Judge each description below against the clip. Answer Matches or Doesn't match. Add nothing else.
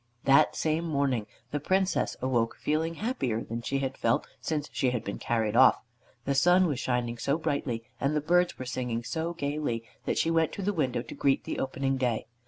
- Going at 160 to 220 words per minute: Matches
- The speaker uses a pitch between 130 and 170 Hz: Matches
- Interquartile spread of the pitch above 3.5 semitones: Matches